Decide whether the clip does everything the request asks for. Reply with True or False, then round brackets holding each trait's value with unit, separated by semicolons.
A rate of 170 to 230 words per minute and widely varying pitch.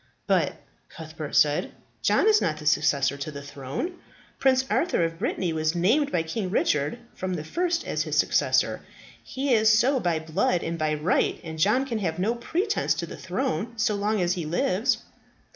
True (185 wpm; 7.6 semitones)